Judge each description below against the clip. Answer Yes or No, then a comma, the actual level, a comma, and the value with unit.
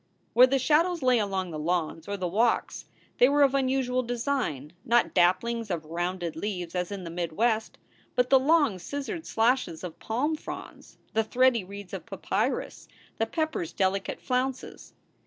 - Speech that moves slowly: No, average, 170 wpm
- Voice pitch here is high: Yes, high, 225 Hz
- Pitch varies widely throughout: Yes, wide, 6.3 semitones